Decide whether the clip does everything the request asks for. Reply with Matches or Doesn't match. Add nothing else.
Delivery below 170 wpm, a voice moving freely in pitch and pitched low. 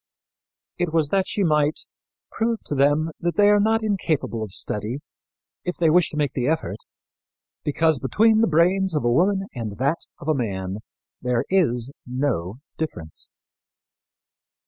Doesn't match